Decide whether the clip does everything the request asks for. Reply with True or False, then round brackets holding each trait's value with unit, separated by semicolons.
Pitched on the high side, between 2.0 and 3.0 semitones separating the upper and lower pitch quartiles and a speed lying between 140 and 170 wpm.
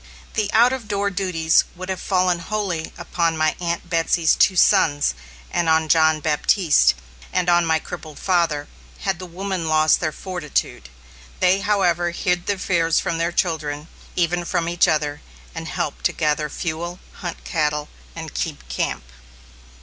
False (170 Hz; 2.6 semitones; 155 wpm)